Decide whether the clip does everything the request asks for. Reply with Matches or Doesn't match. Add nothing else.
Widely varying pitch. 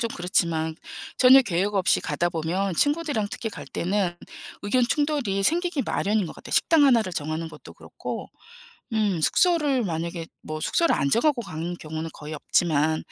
Matches